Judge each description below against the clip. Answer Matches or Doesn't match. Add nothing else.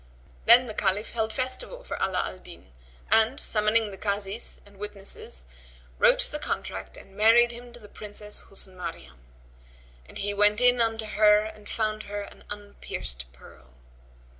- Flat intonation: Matches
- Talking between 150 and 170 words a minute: Matches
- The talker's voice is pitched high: Matches